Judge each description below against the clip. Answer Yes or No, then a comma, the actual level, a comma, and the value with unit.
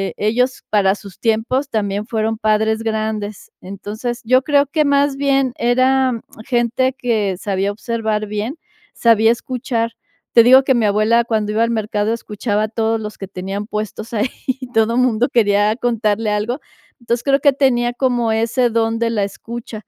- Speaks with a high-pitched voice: Yes, high, 225 Hz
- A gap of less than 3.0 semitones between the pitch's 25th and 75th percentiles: Yes, narrow, 2.6 semitones